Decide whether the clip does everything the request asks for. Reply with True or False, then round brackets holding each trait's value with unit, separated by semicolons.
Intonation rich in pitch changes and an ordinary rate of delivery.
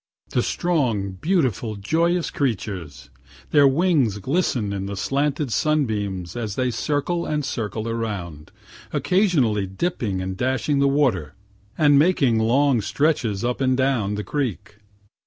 False (6.3 semitones; 130 wpm)